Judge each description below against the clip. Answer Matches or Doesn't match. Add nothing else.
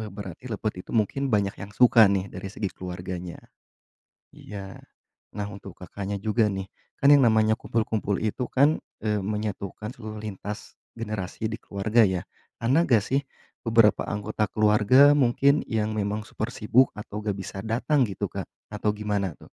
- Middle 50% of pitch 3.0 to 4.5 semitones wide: Doesn't match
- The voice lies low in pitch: Matches